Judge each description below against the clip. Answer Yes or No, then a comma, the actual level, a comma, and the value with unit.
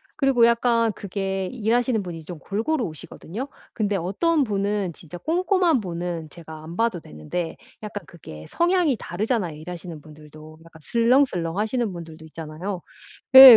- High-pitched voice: Yes, high, 195 Hz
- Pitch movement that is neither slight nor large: No, wide, 6.1 semitones